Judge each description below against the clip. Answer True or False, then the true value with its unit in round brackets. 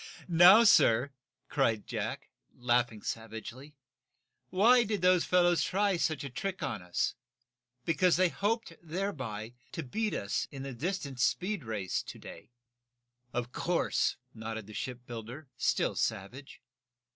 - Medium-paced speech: False (130 wpm)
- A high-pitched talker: False (140 Hz)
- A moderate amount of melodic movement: False (8.0 semitones)